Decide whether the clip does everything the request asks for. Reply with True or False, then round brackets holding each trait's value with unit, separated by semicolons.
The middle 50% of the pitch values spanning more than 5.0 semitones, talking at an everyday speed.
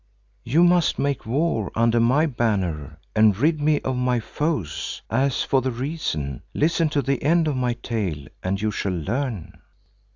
True (5.5 semitones; 165 wpm)